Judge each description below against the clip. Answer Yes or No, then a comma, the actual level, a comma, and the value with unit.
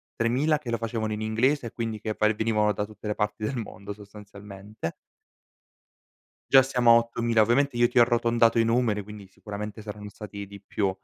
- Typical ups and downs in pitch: No, narrow, 2.1 semitones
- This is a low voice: Yes, low, 110 Hz